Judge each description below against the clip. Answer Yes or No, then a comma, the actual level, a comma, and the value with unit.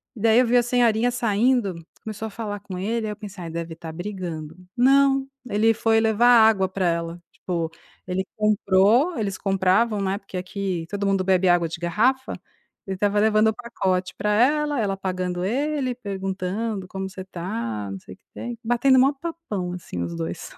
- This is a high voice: Yes, high, 200 Hz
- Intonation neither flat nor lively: Yes, average, 4.0 semitones